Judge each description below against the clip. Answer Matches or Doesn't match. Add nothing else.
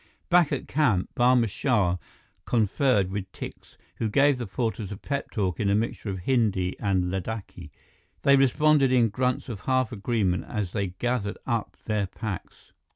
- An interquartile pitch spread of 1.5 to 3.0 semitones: Doesn't match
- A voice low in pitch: Matches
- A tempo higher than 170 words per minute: Doesn't match